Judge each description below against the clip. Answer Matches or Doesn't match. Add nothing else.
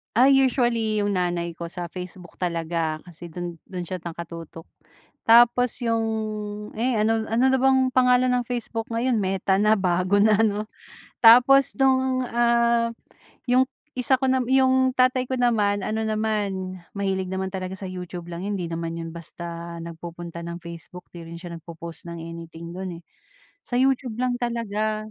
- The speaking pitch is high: Matches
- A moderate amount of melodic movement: Doesn't match